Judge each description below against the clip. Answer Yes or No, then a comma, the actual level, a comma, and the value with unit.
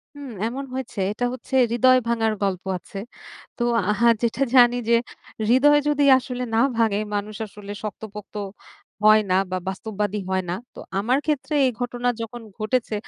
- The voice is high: Yes, high, 230 Hz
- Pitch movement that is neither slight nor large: Yes, average, 3.3 semitones